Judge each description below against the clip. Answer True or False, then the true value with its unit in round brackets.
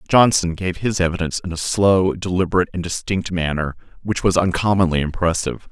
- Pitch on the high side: False (90 Hz)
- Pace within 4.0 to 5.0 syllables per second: False (5.9 syllables/s)